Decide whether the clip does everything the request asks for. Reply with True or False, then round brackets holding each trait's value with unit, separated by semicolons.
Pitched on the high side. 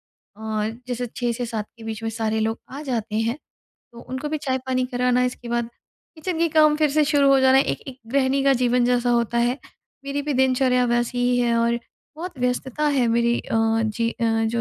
True (245 Hz)